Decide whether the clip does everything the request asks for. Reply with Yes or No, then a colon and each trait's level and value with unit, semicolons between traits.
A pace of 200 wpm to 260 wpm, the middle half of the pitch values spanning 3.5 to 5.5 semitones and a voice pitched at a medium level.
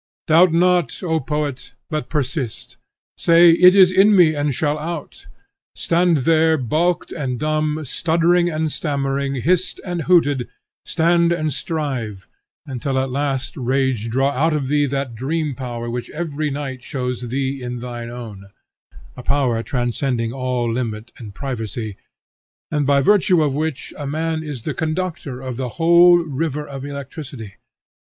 No: average, 150 wpm; average, 4.2 semitones; medium, 145 Hz